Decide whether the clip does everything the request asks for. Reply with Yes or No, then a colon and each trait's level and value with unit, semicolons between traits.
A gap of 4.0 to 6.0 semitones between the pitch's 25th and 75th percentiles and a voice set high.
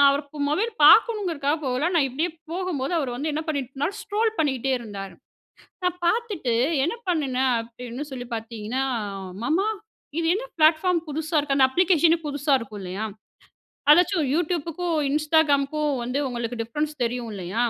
Yes: average, 5.2 semitones; very high, 295 Hz